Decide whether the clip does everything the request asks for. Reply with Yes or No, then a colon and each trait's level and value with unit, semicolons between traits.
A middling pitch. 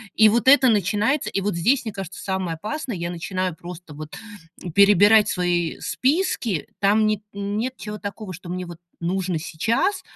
No: high, 200 Hz